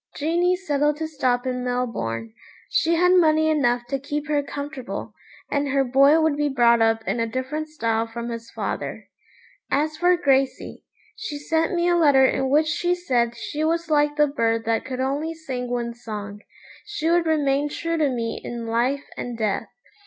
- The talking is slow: No, average, 180 wpm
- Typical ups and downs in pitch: Yes, average, 4.6 semitones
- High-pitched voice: Yes, very high, 280 Hz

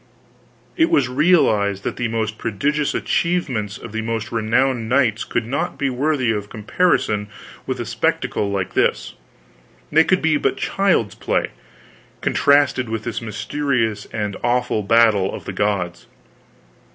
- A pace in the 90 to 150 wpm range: Yes, average, 140 wpm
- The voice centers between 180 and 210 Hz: No, low, 115 Hz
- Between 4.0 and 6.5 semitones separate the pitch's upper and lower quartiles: Yes, average, 5.1 semitones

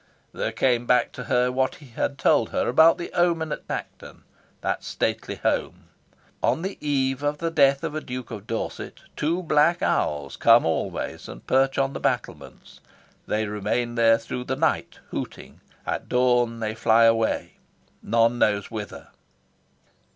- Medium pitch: No, low, 125 Hz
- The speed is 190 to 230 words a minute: No, average, 160 wpm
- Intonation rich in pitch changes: No, average, 4.3 semitones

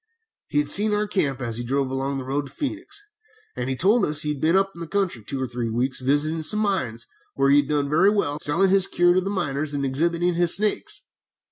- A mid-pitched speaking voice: Yes, medium, 150 Hz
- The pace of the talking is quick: Yes, fast, 240 wpm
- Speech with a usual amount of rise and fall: No, wide, 6.0 semitones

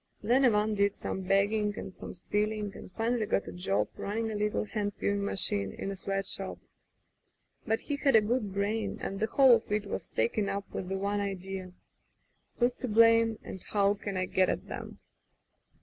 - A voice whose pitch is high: Yes, high, 205 Hz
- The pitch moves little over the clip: Yes, narrow, 2.1 semitones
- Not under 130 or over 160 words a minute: No, average, 195 wpm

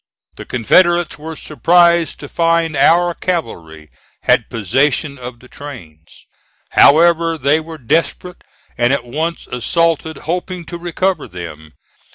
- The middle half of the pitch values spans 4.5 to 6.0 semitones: Yes, wide, 5.5 semitones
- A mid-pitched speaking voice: Yes, medium, 155 Hz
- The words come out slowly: Yes, slow, 125 wpm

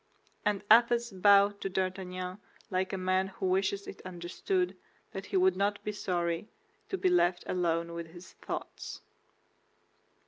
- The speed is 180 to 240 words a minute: No, average, 145 wpm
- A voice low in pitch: No, high, 190 Hz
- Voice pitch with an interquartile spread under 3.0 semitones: Yes, narrow, 2.4 semitones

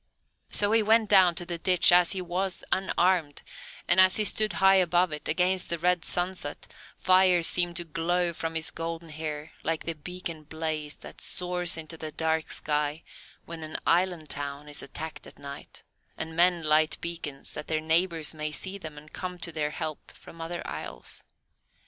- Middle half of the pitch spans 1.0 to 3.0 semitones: Yes, narrow, 2.5 semitones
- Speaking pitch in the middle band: Yes, medium, 165 Hz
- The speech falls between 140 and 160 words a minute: No, average, 180 wpm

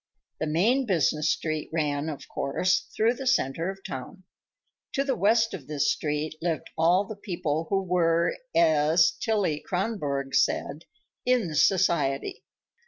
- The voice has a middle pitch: Yes, medium, 165 Hz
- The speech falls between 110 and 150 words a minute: Yes, average, 145 wpm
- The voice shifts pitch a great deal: No, average, 4.6 semitones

